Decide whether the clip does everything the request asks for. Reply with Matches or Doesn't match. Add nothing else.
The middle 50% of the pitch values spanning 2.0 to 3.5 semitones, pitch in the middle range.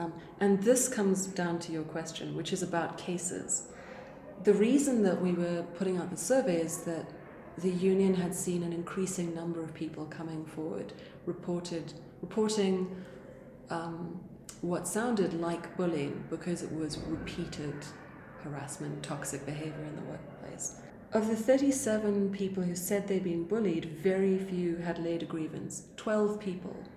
Matches